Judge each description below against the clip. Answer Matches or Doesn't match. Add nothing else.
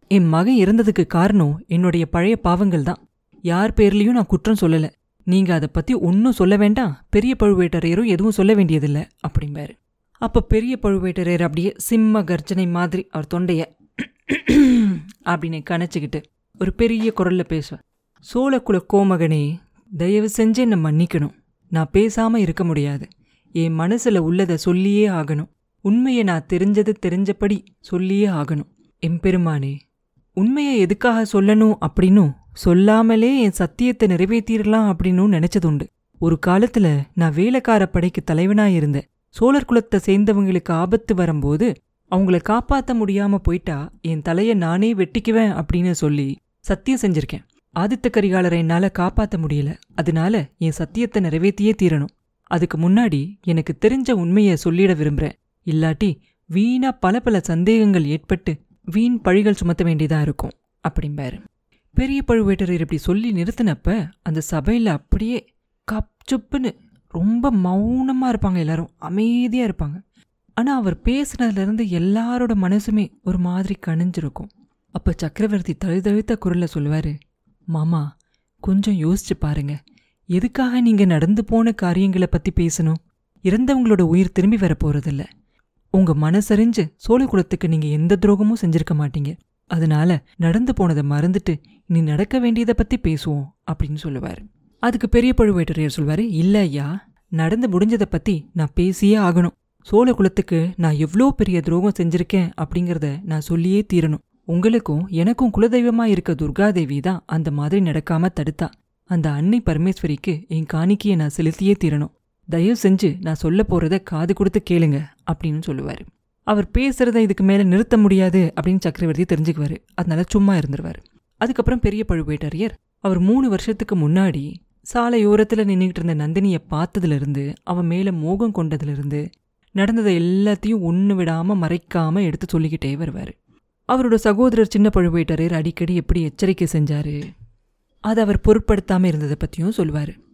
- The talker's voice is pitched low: Doesn't match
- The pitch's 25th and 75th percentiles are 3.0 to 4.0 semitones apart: Doesn't match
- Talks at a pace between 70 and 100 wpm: Doesn't match